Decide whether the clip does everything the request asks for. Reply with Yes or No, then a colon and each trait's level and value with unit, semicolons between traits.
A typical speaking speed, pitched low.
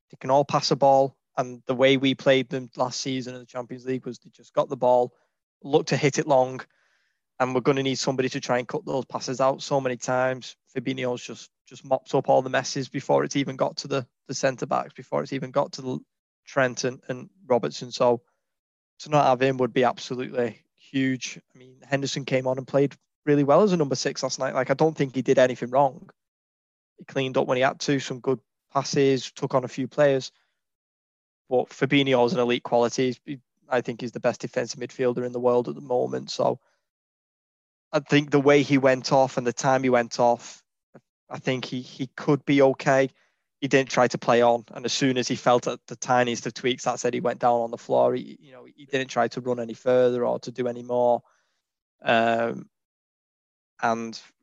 No: fast, 220 wpm; low, 130 Hz